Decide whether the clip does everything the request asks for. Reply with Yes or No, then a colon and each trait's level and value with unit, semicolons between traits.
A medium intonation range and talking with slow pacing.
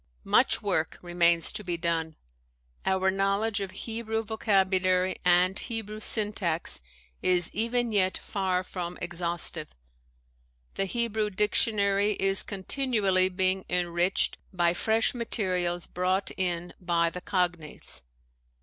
Yes: average, 3.0 semitones; slow, 115 wpm